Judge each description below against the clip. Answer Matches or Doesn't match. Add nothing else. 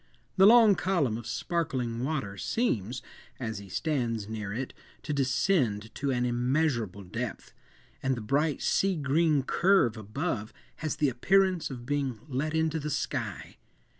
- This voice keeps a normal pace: Matches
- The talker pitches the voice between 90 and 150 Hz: Matches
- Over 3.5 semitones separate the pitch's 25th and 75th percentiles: Matches